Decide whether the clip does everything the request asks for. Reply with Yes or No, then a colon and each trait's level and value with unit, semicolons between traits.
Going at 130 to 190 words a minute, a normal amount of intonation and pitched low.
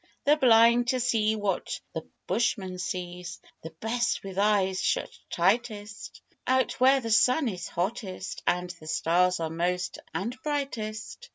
No: average, 140 wpm; average, 4.9 semitones; high, 210 Hz